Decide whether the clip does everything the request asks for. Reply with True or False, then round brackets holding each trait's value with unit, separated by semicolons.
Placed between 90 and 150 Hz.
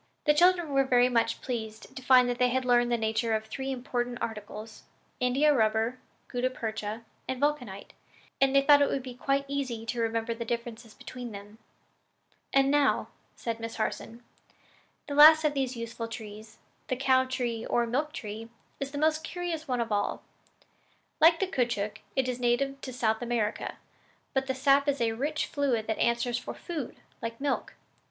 False (245 Hz)